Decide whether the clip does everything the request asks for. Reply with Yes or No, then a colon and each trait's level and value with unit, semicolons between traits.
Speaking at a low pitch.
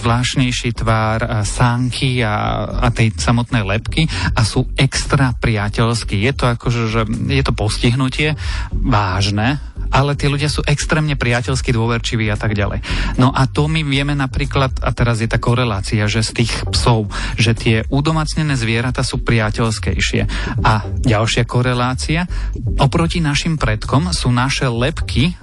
Yes: low, 120 Hz